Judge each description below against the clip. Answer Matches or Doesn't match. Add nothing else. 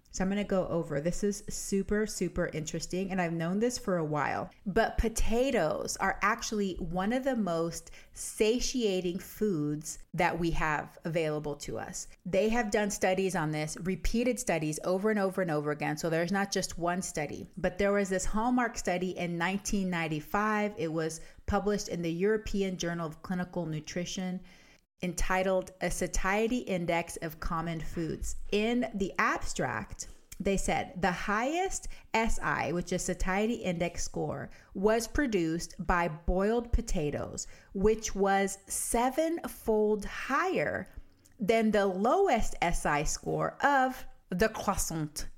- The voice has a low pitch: Doesn't match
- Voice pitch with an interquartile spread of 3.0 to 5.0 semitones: Matches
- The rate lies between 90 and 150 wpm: Matches